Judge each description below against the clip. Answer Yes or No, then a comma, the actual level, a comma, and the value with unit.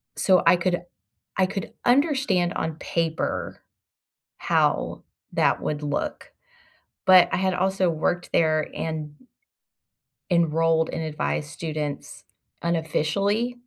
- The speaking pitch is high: No, medium, 170 Hz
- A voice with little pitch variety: No, average, 3.1 semitones